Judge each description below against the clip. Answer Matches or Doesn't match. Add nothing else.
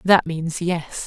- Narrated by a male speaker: Doesn't match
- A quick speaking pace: Doesn't match